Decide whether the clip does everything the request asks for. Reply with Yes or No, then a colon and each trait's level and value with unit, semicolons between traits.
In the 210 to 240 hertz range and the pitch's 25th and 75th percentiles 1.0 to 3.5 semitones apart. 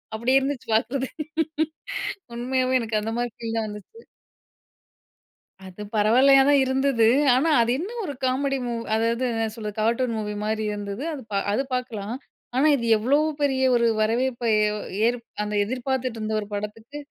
Yes: high, 235 Hz; average, 3.2 semitones